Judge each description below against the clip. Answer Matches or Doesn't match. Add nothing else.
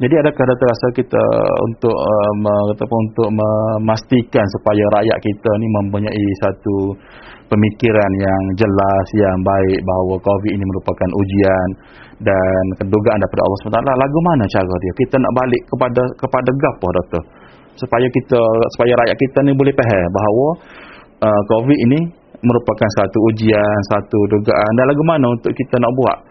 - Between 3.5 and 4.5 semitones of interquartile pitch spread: Matches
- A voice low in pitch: Matches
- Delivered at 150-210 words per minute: Matches